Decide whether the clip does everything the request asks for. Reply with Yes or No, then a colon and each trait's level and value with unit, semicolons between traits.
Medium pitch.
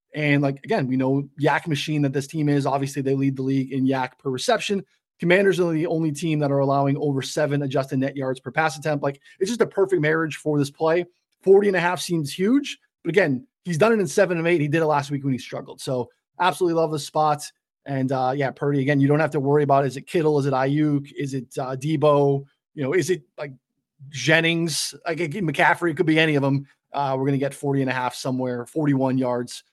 Yes: medium, 145 Hz